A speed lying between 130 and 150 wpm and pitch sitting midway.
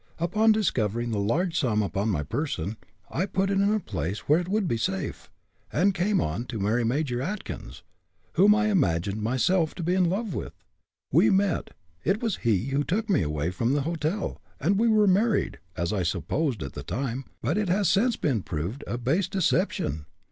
No: average, 195 wpm; medium, 150 Hz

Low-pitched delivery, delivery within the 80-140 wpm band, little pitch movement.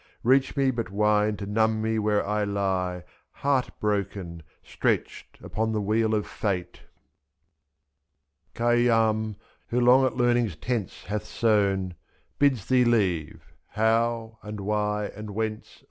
Yes: low, 110 Hz; slow, 135 wpm; narrow, 2.3 semitones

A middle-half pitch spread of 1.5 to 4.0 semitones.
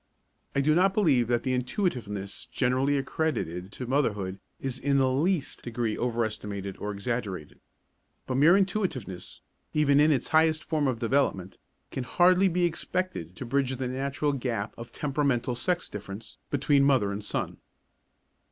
No: average, 4.9 semitones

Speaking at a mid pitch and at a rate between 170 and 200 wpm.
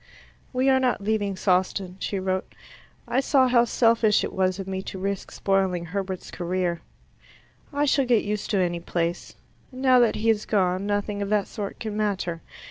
No: high, 200 Hz; average, 180 wpm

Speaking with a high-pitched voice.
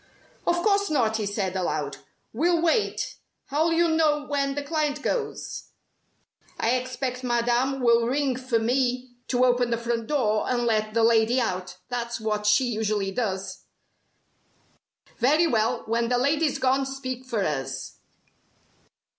Yes: high, 245 Hz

